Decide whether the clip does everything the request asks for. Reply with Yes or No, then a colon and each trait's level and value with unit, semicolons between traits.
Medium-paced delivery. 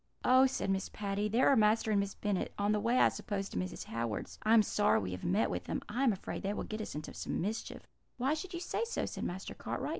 No: fast, 265 wpm